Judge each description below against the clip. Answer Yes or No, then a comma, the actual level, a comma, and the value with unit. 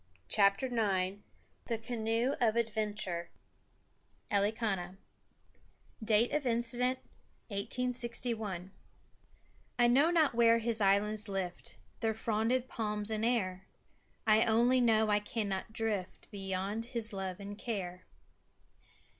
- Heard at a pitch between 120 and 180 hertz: No, high, 220 Hz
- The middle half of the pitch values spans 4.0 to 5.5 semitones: No, average, 2.9 semitones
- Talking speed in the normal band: No, slow, 110 wpm